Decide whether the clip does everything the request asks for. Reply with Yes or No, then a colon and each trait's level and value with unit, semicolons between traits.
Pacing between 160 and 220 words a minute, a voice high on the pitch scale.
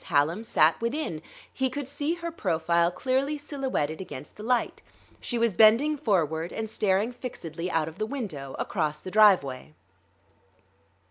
No: average, 145 wpm; high, 210 Hz